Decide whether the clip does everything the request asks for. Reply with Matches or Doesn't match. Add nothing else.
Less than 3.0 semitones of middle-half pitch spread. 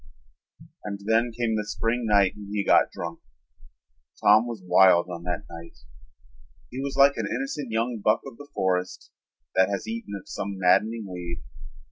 Doesn't match